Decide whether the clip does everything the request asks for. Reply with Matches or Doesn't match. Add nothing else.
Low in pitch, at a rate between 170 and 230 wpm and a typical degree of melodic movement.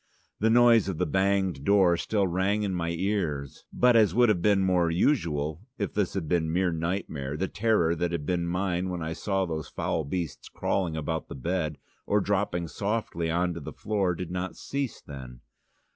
Matches